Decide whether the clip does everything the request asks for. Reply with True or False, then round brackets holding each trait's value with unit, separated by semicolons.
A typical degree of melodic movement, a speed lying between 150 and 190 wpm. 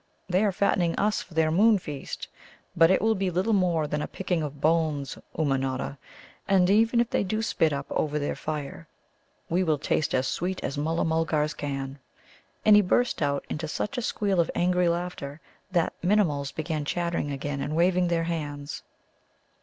True (4.1 semitones; 180 wpm)